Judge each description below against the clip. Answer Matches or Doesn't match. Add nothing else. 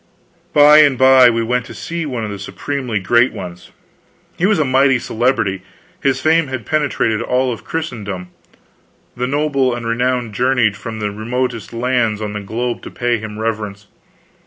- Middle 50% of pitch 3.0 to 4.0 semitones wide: Matches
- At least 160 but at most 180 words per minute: Matches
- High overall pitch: Doesn't match